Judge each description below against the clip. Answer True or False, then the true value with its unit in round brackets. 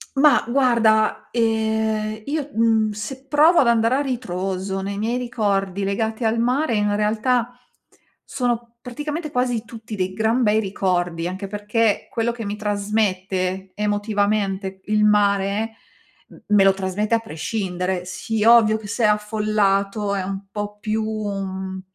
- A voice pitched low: False (215 Hz)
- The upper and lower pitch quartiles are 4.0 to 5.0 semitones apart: False (2.6 semitones)